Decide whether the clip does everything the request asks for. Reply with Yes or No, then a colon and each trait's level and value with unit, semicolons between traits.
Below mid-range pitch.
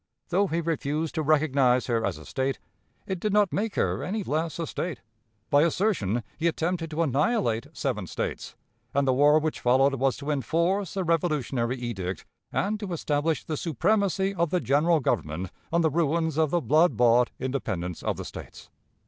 No: medium, 155 Hz